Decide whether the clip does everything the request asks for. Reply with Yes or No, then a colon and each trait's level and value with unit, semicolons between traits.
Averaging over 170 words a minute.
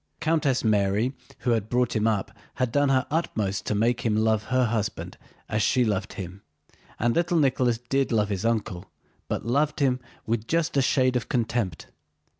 Yes: average, 180 wpm